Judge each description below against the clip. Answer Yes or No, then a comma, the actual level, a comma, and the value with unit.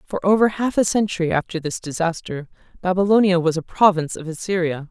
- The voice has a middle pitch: Yes, medium, 180 Hz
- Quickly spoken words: No, average, 170 wpm